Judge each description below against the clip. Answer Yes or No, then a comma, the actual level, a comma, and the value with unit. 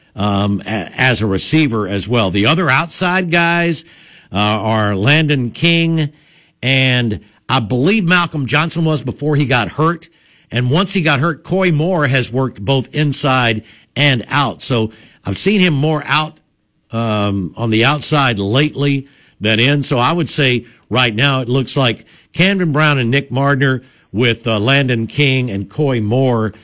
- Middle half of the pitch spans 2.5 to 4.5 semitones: No, average, 5.3 semitones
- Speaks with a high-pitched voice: No, low, 135 Hz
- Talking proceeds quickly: No, average, 160 wpm